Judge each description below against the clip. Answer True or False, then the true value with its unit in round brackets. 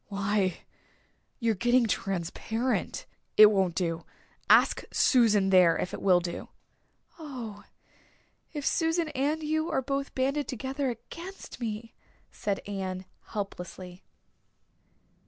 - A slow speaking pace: True (110 wpm)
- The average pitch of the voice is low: False (220 Hz)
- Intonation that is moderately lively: False (6.1 semitones)